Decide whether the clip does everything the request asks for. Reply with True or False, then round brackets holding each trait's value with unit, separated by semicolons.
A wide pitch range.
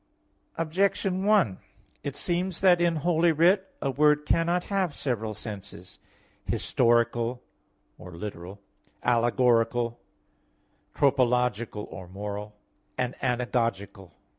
True (7.8 semitones)